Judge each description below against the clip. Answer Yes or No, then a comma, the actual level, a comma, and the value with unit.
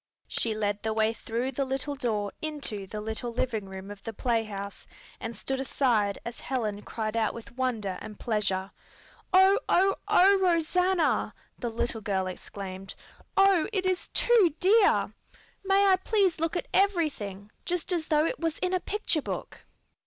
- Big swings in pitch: Yes, wide, 9.0 semitones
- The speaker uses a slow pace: No, average, 165 wpm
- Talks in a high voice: Yes, very high, 250 Hz